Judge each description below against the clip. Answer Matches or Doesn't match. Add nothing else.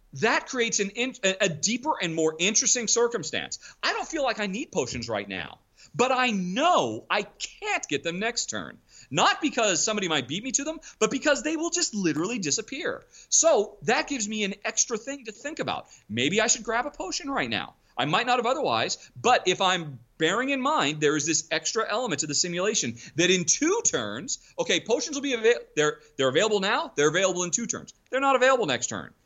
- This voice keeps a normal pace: Doesn't match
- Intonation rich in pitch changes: Matches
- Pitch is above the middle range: Matches